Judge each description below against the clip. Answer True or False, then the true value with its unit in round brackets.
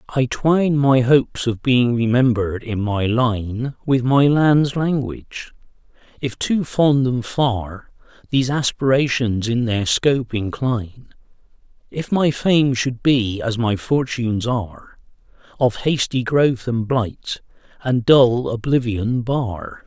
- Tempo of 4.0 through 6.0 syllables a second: False (3.8 syllables/s)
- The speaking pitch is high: False (125 Hz)